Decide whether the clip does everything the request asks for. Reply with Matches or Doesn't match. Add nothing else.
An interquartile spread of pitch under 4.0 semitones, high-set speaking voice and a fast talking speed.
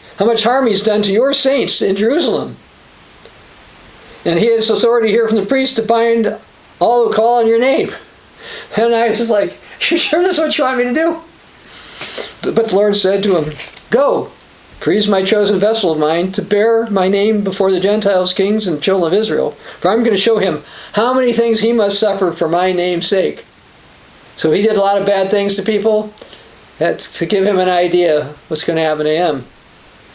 Matches